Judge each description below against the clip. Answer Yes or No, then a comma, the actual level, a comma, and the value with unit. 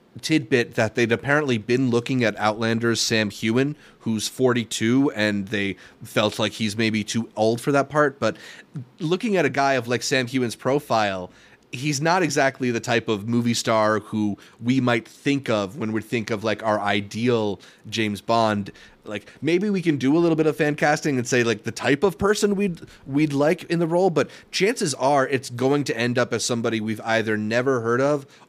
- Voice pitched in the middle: No, low, 120 Hz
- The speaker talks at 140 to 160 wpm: No, average, 200 wpm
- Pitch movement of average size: Yes, average, 4.2 semitones